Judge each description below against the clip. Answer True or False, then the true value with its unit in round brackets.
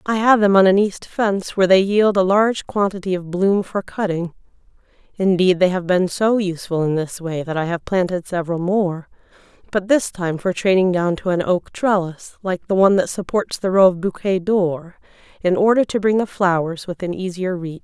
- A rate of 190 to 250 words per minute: True (205 wpm)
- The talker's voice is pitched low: False (185 Hz)